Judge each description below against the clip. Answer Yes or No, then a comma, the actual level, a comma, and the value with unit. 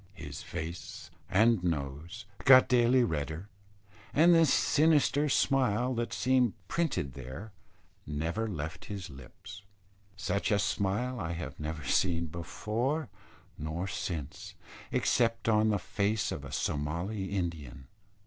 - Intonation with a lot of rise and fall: Yes, wide, 6.9 semitones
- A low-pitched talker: Yes, very low, 95 Hz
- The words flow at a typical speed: No, slow, 120 wpm